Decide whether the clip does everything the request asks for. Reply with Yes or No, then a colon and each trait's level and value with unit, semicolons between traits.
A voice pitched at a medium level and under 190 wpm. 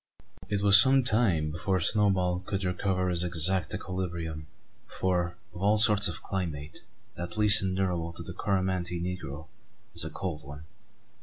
No: very low, 90 Hz; average, 150 wpm